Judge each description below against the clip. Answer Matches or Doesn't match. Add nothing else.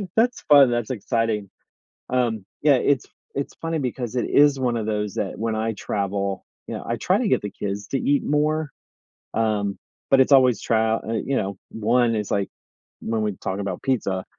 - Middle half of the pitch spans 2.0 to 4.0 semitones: Doesn't match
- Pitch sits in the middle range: Doesn't match